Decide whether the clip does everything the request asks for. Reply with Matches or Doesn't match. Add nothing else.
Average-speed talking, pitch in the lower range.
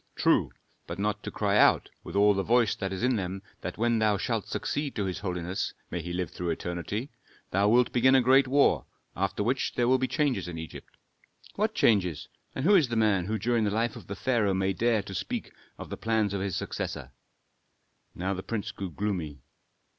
Doesn't match